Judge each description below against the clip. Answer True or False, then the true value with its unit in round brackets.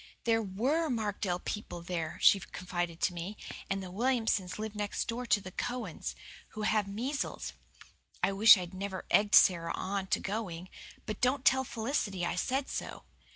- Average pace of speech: True (165 wpm)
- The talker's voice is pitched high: True (205 Hz)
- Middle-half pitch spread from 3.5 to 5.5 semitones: True (3.8 semitones)